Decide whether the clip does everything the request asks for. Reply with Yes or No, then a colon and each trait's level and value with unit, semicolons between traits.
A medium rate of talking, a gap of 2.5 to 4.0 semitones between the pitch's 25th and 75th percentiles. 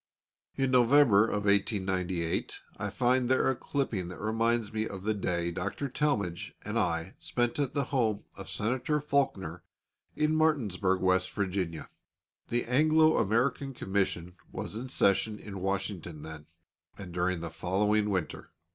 No: average, 145 wpm; average, 5.3 semitones